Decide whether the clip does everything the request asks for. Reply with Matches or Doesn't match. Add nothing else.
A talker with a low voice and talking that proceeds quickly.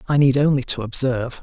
Matches